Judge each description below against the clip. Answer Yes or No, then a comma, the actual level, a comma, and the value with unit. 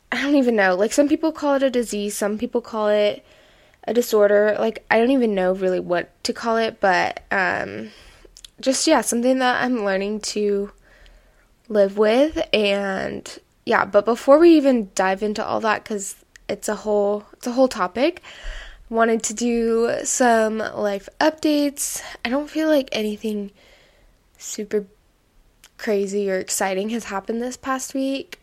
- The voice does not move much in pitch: No, average, 4.3 semitones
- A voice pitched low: No, high, 225 Hz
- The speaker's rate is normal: Yes, average, 160 wpm